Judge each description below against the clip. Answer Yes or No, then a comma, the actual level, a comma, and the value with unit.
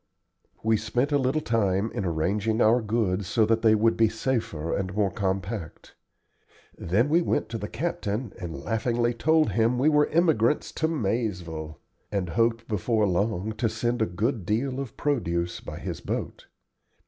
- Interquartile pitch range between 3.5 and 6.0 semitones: Yes, average, 3.8 semitones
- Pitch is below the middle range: Yes, low, 110 Hz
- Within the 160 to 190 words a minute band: Yes, average, 165 wpm